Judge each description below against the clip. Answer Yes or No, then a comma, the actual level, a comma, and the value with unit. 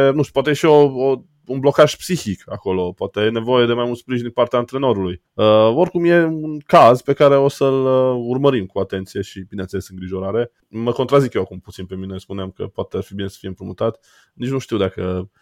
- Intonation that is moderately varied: No, wide, 6.1 semitones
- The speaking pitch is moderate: No, low, 120 Hz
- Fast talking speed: Yes, fast, 220 wpm